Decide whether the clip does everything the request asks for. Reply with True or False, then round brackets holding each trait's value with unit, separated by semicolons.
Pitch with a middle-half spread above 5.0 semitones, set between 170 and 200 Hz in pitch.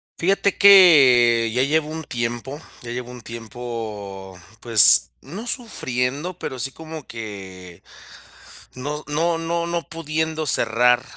False (5.5 semitones; 130 Hz)